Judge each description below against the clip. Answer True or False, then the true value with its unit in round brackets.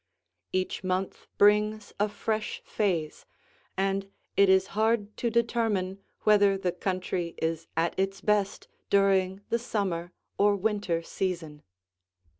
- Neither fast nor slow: False (120 wpm)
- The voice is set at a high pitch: True (195 Hz)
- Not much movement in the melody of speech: True (2.3 semitones)